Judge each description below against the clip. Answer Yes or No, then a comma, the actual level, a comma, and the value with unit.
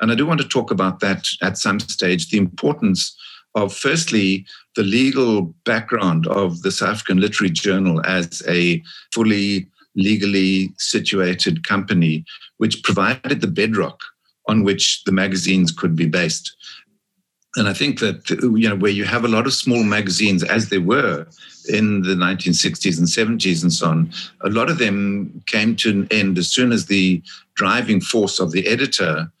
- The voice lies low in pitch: Yes, low, 100 Hz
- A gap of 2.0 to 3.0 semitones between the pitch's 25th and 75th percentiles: No, average, 3.4 semitones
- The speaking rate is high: No, average, 170 wpm